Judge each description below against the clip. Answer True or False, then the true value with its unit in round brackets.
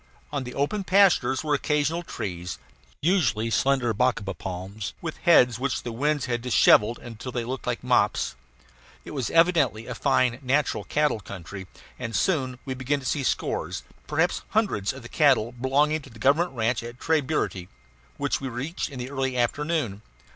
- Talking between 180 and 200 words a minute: False (170 wpm)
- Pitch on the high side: False (130 Hz)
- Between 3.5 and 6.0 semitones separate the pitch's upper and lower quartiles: True (4.3 semitones)